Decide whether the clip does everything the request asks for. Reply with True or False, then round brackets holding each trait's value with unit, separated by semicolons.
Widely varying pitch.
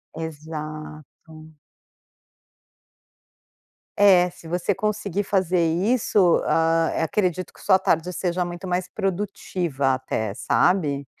False (3.1 semitones)